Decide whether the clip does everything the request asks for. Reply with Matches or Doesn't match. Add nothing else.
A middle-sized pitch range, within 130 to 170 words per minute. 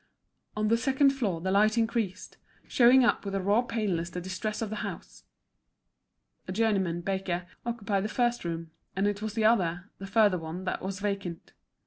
Doesn't match